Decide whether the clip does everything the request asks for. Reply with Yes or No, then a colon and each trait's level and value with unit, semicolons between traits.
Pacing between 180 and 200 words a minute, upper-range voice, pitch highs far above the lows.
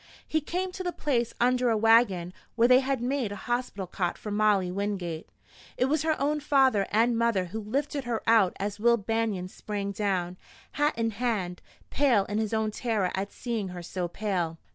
No: average, 190 wpm; high, 220 Hz; average, 4.2 semitones